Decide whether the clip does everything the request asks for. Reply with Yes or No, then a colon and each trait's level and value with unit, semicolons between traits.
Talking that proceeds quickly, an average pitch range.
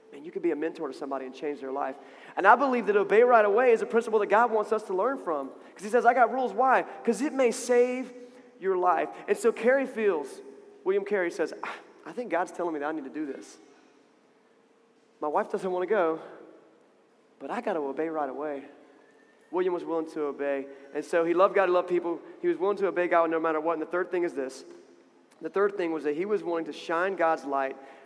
No: fast, 240 wpm; wide, 6.9 semitones